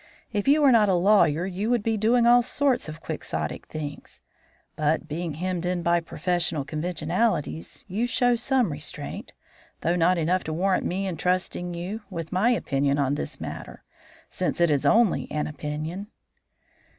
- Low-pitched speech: No, medium, 180 Hz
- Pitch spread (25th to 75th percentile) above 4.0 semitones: Yes, average, 5.3 semitones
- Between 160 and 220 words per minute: Yes, average, 165 wpm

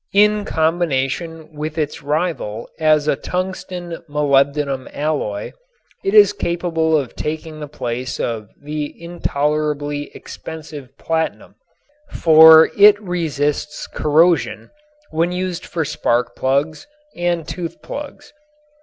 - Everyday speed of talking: No, slow, 110 wpm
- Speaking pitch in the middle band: Yes, medium, 155 Hz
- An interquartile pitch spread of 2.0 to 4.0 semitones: Yes, average, 3.0 semitones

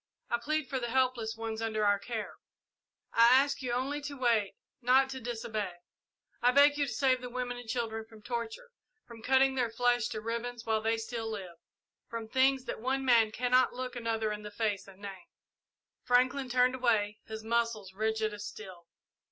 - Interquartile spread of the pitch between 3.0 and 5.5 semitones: No, narrow, 2.6 semitones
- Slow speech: No, average, 185 wpm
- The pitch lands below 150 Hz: No, high, 235 Hz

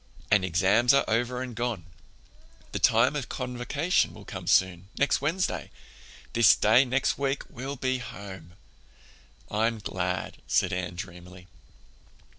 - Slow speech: Yes, slow, 120 wpm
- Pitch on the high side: No, low, 115 Hz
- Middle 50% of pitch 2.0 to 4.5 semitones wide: No, wide, 5.6 semitones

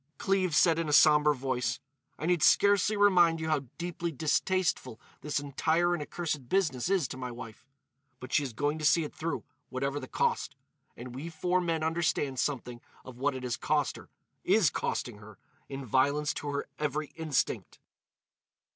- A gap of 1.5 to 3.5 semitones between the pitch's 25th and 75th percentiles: No, average, 4.2 semitones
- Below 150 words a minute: No, average, 170 wpm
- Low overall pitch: No, medium, 150 Hz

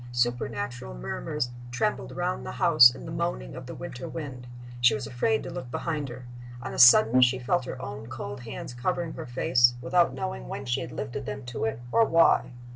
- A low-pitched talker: Yes, low, 120 Hz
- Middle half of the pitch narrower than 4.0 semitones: Yes, average, 2.8 semitones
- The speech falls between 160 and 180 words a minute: No, average, 200 wpm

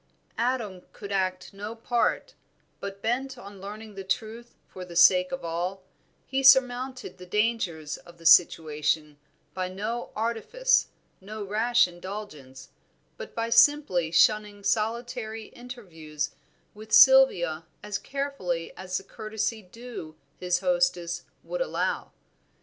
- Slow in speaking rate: Yes, slow, 125 wpm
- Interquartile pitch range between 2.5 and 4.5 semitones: No, average, 5.0 semitones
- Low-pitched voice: No, high, 210 Hz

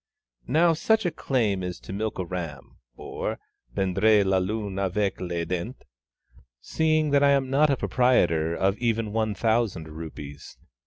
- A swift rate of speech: No, average, 155 wpm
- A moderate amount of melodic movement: No, wide, 6.0 semitones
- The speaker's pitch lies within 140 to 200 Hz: No, low, 105 Hz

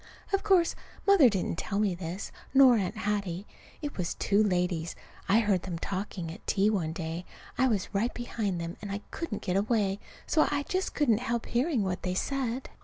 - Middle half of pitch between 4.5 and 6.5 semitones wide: Yes, average, 4.9 semitones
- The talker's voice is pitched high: Yes, high, 205 Hz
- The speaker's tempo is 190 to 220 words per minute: Yes, average, 195 wpm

